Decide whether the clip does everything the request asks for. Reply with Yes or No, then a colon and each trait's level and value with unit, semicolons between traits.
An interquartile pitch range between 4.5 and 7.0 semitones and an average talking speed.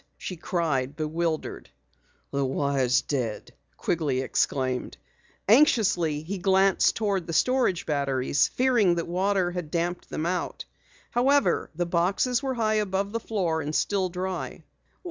No: average, 5.0 semitones; slow, 130 wpm